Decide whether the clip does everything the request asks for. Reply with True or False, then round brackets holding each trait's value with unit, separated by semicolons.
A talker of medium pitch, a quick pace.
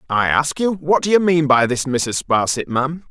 True (145 Hz; 230 wpm)